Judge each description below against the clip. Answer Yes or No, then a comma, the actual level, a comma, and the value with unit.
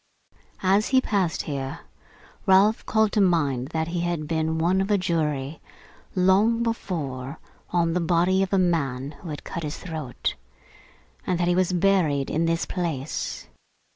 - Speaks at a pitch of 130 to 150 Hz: No, medium, 170 Hz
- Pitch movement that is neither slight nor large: Yes, average, 3.7 semitones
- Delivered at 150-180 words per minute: Yes, average, 160 wpm